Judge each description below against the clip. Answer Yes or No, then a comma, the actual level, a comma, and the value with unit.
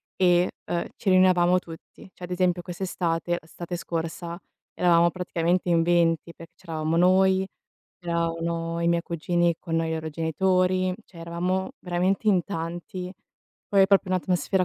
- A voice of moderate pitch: Yes, medium, 175 Hz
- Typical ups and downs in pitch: No, narrow, 1.7 semitones